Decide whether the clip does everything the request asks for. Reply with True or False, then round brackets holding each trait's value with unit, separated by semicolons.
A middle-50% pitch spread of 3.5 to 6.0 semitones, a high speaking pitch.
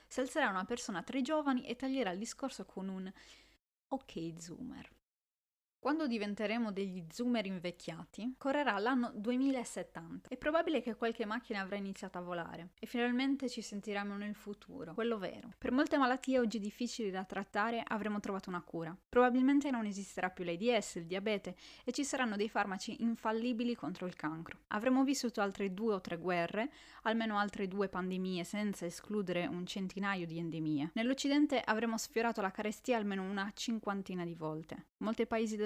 True (4.5 semitones; 210 Hz)